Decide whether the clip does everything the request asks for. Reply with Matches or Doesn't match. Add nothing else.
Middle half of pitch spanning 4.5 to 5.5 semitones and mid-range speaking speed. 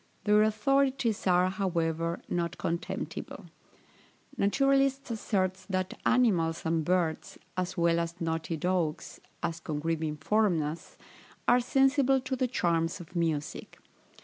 Doesn't match